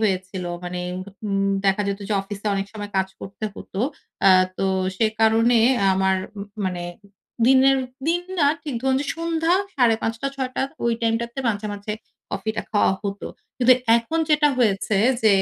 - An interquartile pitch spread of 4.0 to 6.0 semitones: Yes, average, 4.7 semitones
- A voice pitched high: Yes, high, 220 Hz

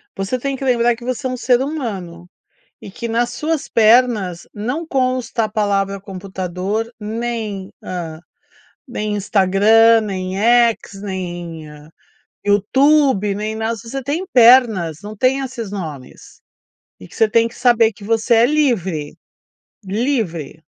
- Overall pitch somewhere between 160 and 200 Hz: No, high, 220 Hz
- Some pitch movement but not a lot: Yes, average, 4.1 semitones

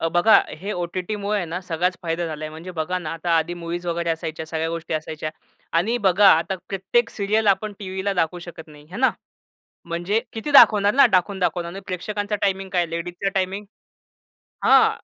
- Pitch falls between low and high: Yes, medium, 180 Hz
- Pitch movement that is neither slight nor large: Yes, average, 3.2 semitones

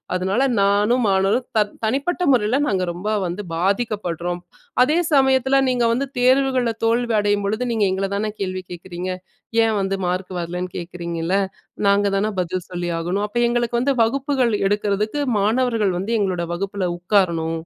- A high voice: Yes, high, 200 Hz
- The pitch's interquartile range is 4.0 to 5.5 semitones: Yes, average, 4.5 semitones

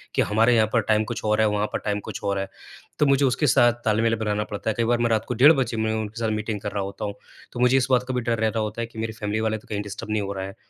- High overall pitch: No, low, 110 Hz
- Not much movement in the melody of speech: Yes, narrow, 2.1 semitones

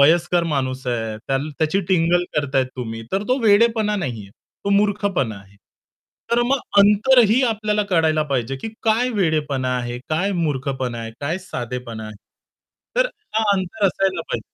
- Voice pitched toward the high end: No, medium, 160 Hz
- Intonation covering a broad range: Yes, wide, 8.0 semitones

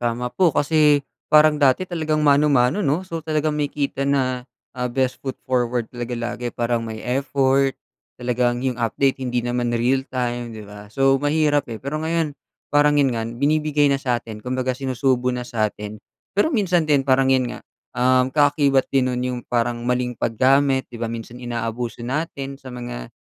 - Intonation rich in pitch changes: No, average, 2.9 semitones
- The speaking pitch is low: Yes, low, 130 Hz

